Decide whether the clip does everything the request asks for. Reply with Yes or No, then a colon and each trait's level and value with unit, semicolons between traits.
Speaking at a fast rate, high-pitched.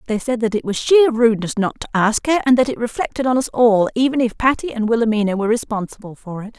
Yes: fast, 245 wpm; high, 230 Hz